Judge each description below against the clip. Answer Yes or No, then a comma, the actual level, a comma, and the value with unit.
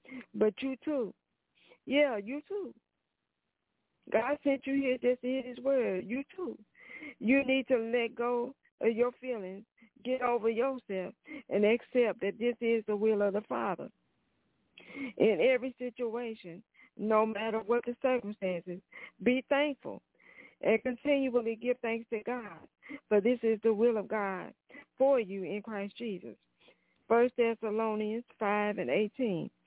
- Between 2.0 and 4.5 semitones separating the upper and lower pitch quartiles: Yes, average, 3.4 semitones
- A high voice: Yes, high, 240 Hz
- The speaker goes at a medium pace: Yes, average, 145 wpm